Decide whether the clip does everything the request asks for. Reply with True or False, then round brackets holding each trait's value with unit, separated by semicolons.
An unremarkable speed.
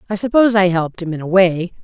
False (260 wpm)